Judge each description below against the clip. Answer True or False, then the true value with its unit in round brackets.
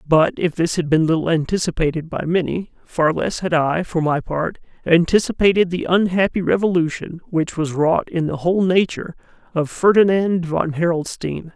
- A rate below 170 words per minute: True (160 wpm)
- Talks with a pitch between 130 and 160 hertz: False (170 Hz)